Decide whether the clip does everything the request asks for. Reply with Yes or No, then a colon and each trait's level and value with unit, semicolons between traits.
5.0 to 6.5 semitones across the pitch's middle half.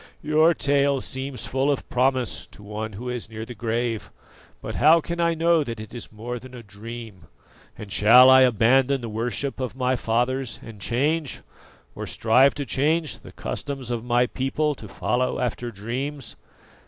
No: average, 3.4 semitones